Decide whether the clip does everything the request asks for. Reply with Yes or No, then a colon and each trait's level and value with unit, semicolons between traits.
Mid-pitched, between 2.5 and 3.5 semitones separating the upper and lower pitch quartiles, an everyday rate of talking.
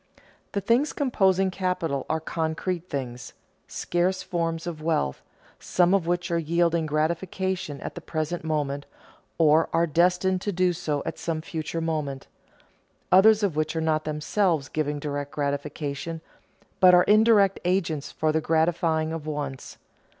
Yes: medium, 165 Hz; average, 2.9 semitones; average, 145 wpm